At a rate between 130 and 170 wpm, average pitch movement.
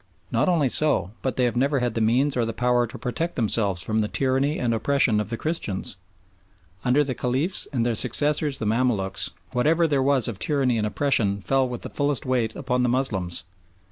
No: average, 200 wpm; average, 3.8 semitones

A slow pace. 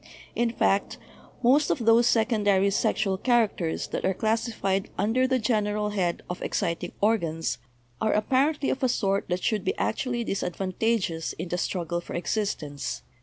No: average, 170 wpm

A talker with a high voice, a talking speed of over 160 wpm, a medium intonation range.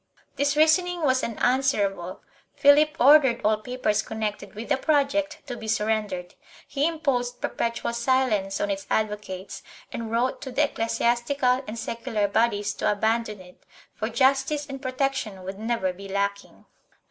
No: high, 235 Hz; average, 145 wpm; average, 4.6 semitones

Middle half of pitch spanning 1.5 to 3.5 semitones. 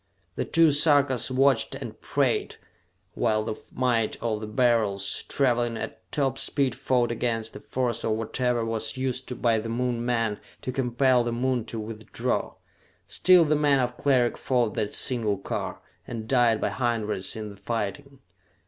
Yes: average, 2.7 semitones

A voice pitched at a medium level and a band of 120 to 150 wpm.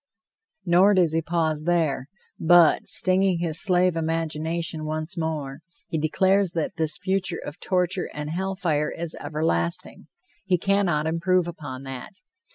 Yes: medium, 165 Hz; average, 140 wpm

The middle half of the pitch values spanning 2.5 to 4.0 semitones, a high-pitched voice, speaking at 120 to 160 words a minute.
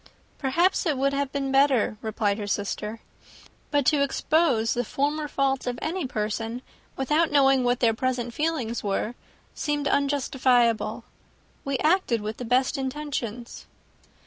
Yes: average, 3.6 semitones; very high, 265 Hz; average, 140 wpm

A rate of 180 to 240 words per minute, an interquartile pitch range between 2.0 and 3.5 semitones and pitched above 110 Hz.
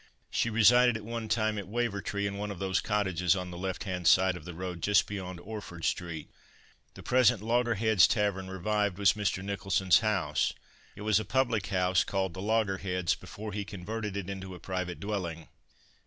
No: average, 185 wpm; average, 2.7 semitones; low, 100 Hz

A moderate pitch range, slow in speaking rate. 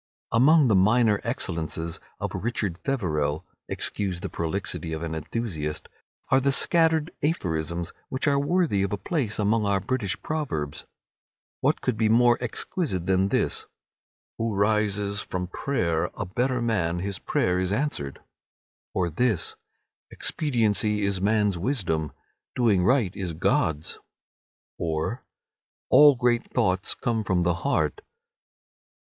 No: wide, 5.9 semitones; slow, 125 wpm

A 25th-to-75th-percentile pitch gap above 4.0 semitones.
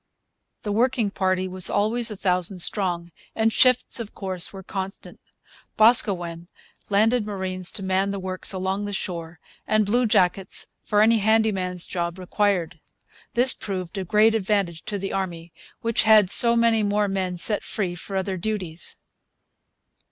No: average, 2.8 semitones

